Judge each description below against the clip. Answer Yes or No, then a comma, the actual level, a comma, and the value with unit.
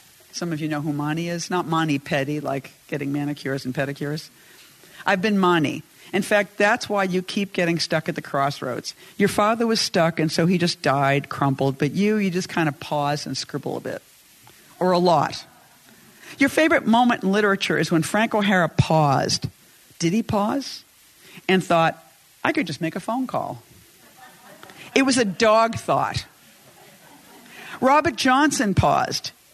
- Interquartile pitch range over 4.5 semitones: Yes, wide, 5.6 semitones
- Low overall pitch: No, medium, 170 Hz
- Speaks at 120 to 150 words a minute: No, average, 170 wpm